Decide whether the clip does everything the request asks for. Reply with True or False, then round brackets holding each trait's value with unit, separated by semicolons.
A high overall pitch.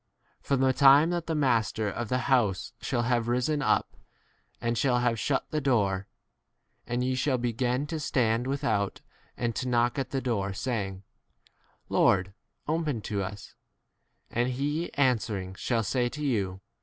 False (120 Hz)